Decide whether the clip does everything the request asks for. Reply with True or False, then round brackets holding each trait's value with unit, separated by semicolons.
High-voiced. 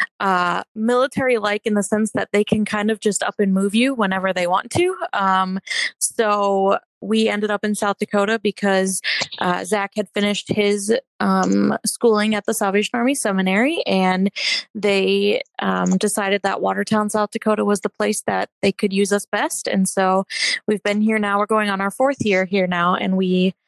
True (205 Hz)